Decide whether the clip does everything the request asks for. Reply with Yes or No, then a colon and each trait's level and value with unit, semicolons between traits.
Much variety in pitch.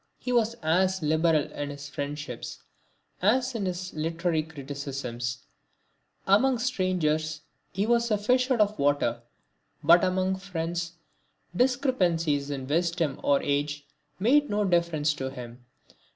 Yes: wide, 5.8 semitones